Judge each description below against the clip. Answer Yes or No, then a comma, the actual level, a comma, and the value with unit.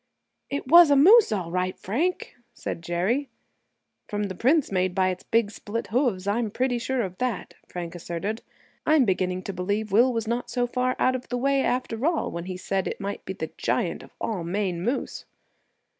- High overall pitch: Yes, high, 215 Hz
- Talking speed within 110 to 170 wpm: No, average, 195 wpm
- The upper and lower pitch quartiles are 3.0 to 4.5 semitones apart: No, wide, 5.5 semitones